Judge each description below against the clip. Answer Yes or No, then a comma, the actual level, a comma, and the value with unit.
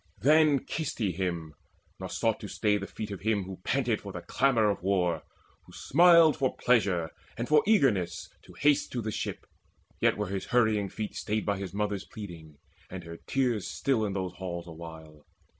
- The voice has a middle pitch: No, low, 100 Hz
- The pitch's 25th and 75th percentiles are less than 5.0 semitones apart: No, wide, 5.5 semitones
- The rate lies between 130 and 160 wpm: No, average, 190 wpm